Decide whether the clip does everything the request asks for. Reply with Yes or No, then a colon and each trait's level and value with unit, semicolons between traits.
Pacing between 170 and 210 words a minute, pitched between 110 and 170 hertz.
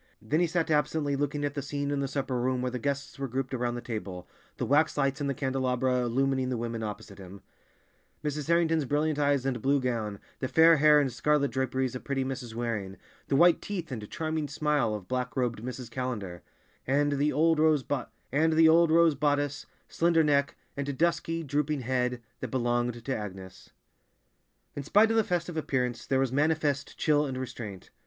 Yes: average, 185 wpm; low, 135 Hz